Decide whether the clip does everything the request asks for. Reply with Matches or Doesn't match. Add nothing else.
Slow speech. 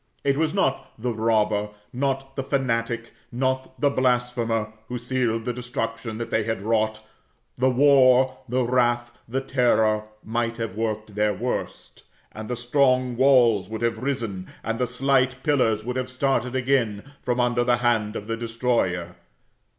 Doesn't match